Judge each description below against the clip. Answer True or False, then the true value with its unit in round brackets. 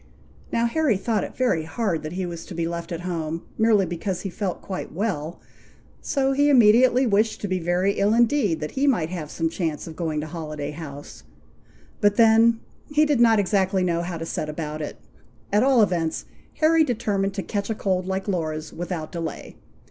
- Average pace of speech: True (195 wpm)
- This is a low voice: False (185 Hz)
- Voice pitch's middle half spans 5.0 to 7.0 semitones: True (5.3 semitones)